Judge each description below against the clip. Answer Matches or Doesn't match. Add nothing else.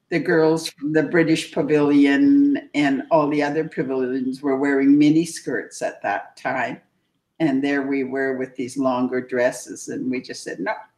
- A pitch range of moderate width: Matches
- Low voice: Doesn't match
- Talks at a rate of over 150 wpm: Matches